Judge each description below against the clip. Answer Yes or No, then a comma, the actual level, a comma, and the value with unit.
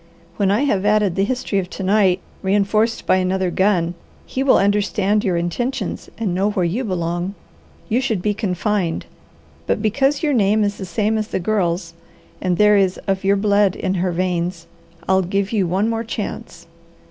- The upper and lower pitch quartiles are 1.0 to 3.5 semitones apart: Yes, narrow, 2.6 semitones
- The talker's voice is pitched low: No, high, 195 Hz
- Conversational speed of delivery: Yes, average, 180 wpm